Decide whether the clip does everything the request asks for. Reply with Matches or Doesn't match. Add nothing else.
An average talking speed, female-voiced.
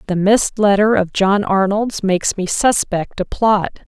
Matches